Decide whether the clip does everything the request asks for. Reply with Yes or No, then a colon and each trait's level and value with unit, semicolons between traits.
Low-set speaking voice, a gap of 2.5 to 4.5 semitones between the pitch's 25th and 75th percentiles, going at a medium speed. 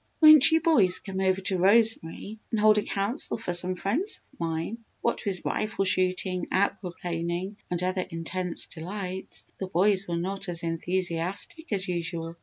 No: medium, 185 Hz; average, 2.9 semitones; average, 165 wpm